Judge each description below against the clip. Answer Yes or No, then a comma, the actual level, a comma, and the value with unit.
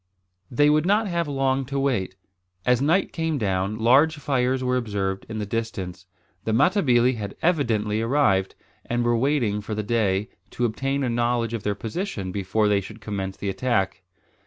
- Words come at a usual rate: Yes, average, 175 wpm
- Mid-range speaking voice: No, low, 115 Hz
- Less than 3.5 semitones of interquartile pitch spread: No, average, 5.0 semitones